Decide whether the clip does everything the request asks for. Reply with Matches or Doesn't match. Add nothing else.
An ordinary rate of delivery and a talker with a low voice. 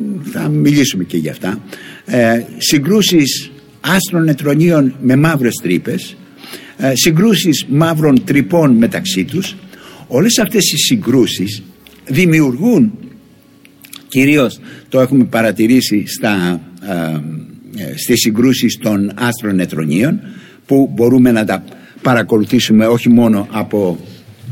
Doesn't match